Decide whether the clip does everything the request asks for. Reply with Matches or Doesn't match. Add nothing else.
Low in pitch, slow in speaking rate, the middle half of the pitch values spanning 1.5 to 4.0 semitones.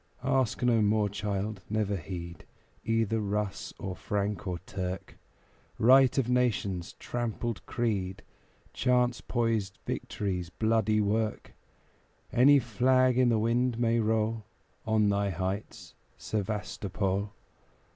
Matches